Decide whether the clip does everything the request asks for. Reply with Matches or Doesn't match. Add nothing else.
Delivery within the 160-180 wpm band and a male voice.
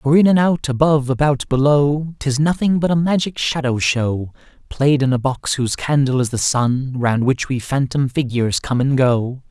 Doesn't match